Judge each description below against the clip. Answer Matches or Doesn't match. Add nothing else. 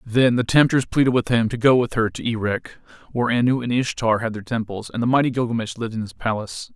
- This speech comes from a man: Matches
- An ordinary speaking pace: Doesn't match